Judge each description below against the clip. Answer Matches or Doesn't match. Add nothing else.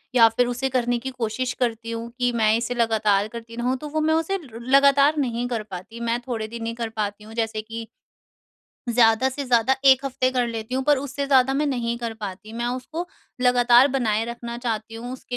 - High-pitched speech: Matches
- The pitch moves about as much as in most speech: Doesn't match